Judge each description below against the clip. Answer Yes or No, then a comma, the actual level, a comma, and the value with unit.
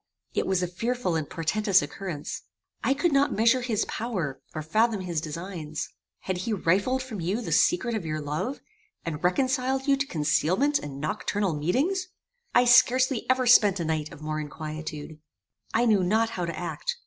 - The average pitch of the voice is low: No, high, 190 Hz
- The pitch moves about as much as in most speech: No, wide, 7.7 semitones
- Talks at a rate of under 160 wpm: No, average, 175 wpm